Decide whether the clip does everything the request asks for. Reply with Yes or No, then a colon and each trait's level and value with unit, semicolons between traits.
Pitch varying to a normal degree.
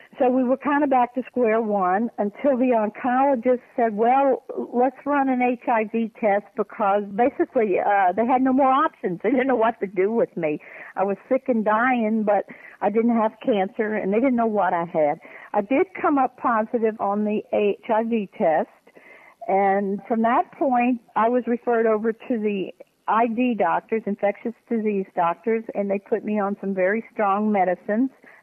Yes: average, 3.7 semitones